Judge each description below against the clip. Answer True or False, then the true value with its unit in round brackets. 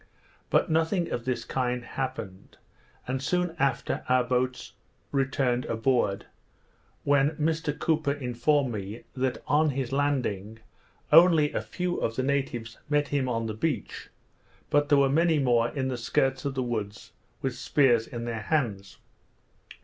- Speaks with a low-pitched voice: True (130 Hz)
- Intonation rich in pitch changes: False (3.5 semitones)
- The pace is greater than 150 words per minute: False (145 wpm)